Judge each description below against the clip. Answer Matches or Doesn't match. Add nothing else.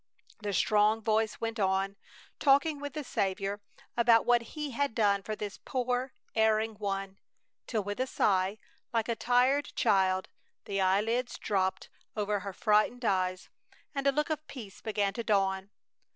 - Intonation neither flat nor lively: Matches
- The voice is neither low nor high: Doesn't match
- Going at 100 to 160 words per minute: Matches